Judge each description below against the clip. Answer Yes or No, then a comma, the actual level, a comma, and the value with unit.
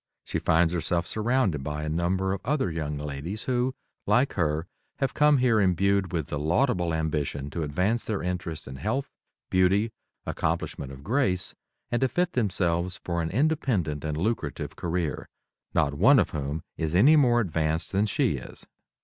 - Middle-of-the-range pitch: No, very low, 90 Hz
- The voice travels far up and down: Yes, wide, 6.7 semitones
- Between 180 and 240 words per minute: No, average, 165 wpm